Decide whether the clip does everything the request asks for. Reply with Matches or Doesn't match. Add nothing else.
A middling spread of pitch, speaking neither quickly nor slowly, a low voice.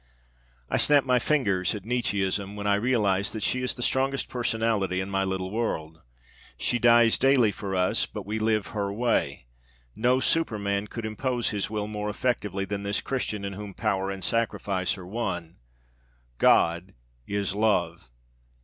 Matches